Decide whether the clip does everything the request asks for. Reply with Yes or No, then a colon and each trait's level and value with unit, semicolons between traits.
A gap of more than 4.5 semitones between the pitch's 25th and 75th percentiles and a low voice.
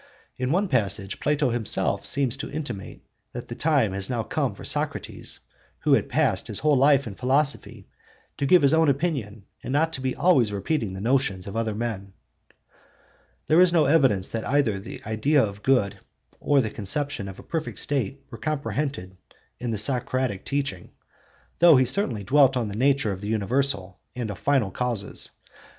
Yes: wide, 5.6 semitones; low, 125 Hz